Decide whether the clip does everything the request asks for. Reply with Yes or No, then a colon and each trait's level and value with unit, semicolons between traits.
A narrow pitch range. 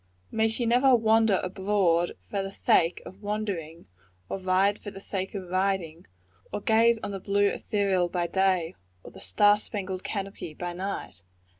Yes: narrow, 2.3 semitones